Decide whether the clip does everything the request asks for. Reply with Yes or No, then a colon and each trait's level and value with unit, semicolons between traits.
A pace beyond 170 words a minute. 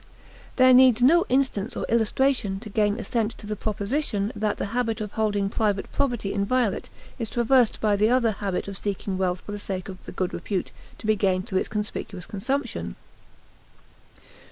Yes: average, 180 wpm